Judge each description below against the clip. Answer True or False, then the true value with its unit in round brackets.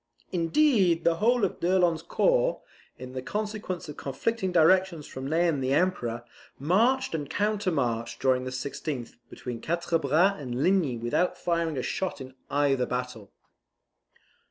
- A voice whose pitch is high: False (165 Hz)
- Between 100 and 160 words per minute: True (140 wpm)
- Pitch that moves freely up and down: True (6.3 semitones)